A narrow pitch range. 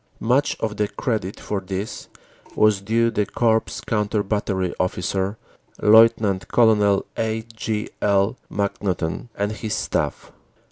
Yes: narrow, 2.2 semitones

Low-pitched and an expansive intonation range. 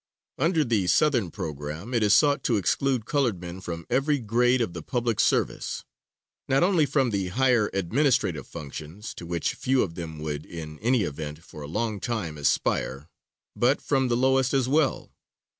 Yes: low, 110 Hz; wide, 7.7 semitones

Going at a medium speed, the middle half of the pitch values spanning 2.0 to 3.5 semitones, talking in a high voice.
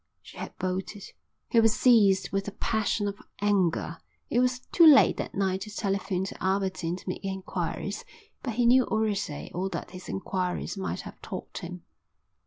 Yes: average, 175 wpm; average, 2.7 semitones; high, 195 Hz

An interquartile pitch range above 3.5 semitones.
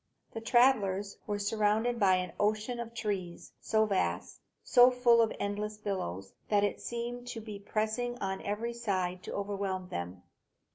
No: average, 3.2 semitones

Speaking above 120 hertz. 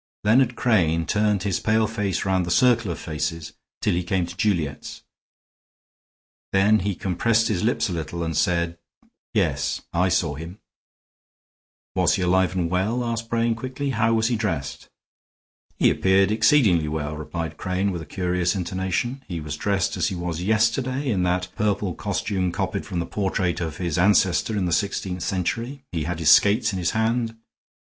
No: very low, 95 Hz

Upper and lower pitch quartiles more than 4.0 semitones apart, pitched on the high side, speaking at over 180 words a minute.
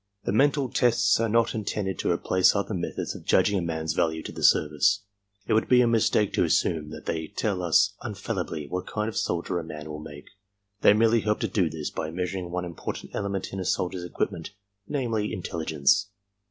No: average, 4.7 semitones; very low, 95 Hz; fast, 205 wpm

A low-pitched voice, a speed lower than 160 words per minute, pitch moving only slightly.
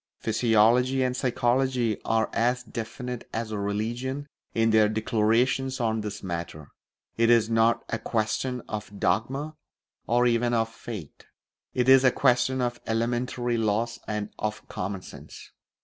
Yes: low, 115 Hz; slow, 135 wpm; narrow, 2.3 semitones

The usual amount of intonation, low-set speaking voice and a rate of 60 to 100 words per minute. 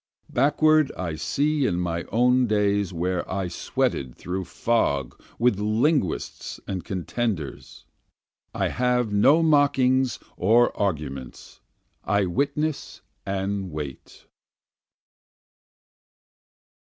No: wide, 6.3 semitones; low, 105 Hz; slow, 90 wpm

